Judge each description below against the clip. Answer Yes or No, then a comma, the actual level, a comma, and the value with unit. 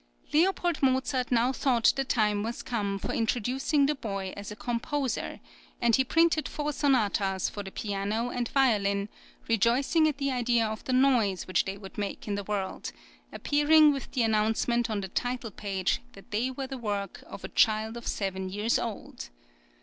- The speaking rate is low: No, average, 180 wpm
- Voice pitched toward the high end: Yes, high, 230 Hz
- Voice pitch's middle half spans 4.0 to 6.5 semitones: Yes, average, 4.4 semitones